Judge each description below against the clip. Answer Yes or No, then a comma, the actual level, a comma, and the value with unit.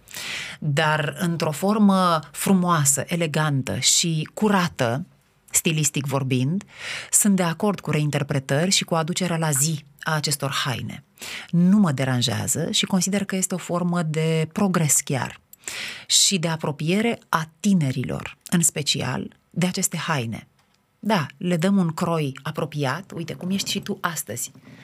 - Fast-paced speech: No, average, 135 wpm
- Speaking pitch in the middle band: Yes, medium, 165 Hz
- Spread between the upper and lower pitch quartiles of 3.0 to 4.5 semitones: Yes, average, 3.8 semitones